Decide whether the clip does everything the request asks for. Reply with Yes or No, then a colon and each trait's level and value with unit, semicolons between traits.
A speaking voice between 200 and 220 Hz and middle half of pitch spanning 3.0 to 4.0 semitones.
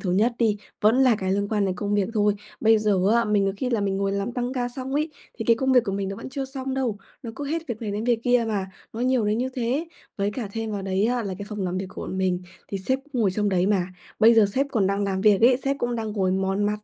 Yes: high, 215 Hz; average, 3.7 semitones